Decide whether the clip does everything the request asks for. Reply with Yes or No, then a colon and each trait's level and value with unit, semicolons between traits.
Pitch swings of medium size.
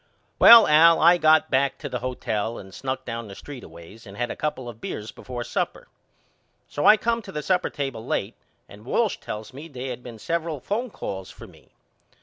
No: wide, 5.8 semitones